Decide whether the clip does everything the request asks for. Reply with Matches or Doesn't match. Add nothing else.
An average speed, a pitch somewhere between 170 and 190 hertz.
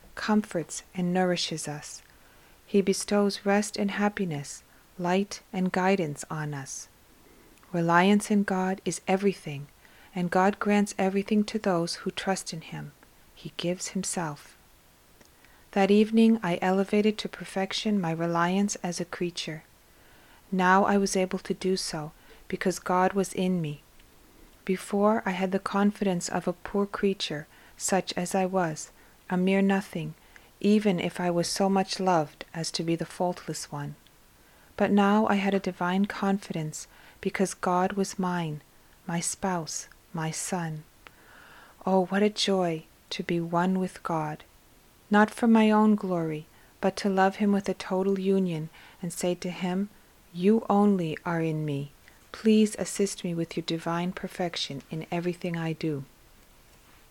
Matches